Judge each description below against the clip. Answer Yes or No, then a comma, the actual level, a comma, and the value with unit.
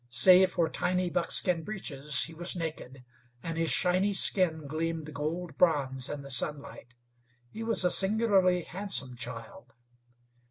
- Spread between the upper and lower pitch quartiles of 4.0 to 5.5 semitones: Yes, average, 4.4 semitones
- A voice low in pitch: No, medium, 165 Hz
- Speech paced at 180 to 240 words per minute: No, slow, 135 wpm